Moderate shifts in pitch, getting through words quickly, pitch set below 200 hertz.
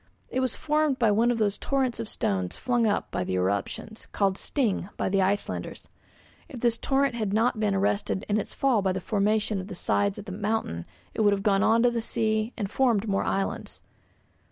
No: average, 3.2 semitones; fast, 210 wpm; high, 215 Hz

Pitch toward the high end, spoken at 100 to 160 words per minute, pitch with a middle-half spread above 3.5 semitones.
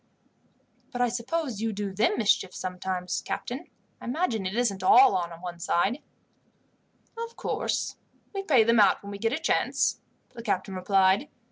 Yes: high, 210 Hz; average, 155 wpm; average, 4.6 semitones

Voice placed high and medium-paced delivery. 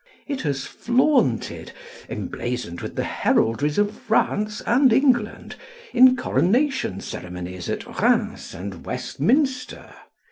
No: high, 210 Hz; slow, 105 wpm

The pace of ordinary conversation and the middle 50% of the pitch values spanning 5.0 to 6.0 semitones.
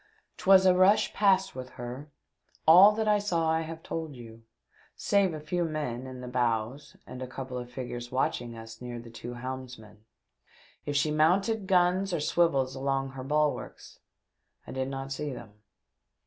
Yes: average, 175 wpm; wide, 5.5 semitones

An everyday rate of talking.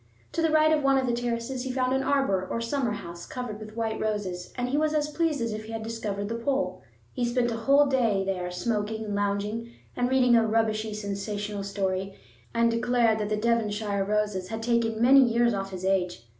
No: fast, 215 wpm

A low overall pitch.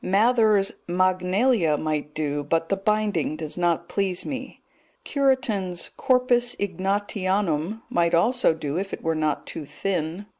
No: medium, 185 Hz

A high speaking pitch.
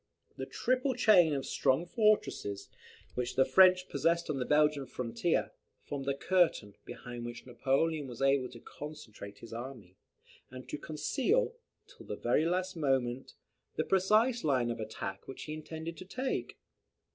No: medium, 145 Hz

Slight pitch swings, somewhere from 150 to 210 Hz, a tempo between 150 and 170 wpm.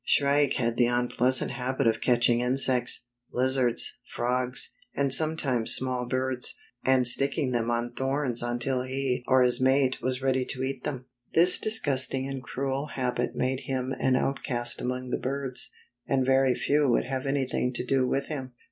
No: narrow, 1.5 semitones; low, 130 Hz; average, 165 wpm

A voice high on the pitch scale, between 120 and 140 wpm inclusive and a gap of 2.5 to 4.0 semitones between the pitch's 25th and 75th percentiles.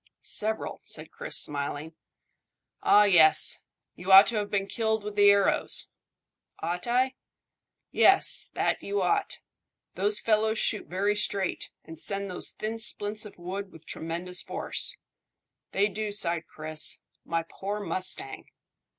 Yes: high, 200 Hz; slow, 135 wpm; average, 3.4 semitones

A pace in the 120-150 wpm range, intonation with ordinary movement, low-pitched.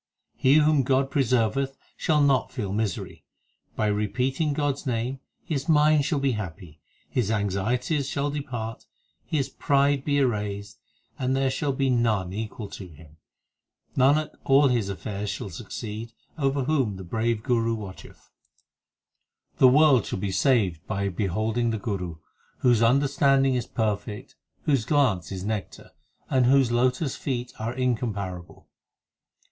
Yes: average, 145 wpm; average, 4.8 semitones; low, 120 Hz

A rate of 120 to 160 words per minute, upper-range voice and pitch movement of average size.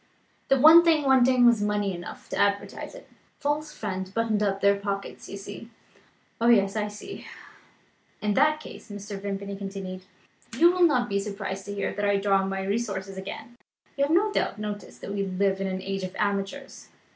No: average, 190 wpm; high, 205 Hz; average, 3.7 semitones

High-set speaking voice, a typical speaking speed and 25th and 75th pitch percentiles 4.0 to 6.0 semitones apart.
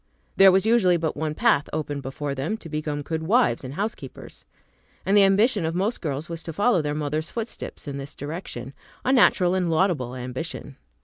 No: medium, 160 Hz; average, 190 wpm; average, 5.0 semitones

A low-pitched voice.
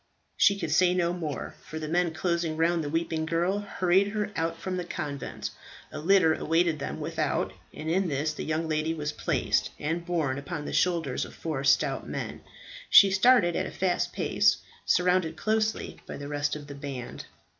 No: medium, 165 Hz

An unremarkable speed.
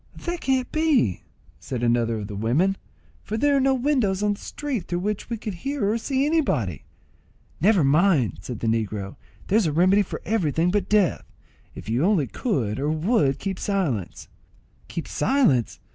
Yes: average, 175 wpm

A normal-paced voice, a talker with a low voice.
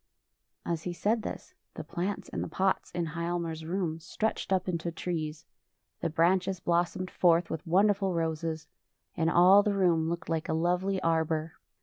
No: average, 165 wpm; medium, 170 Hz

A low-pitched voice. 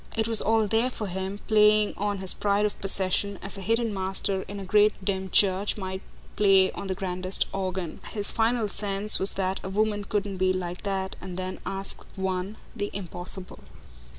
No: high, 195 Hz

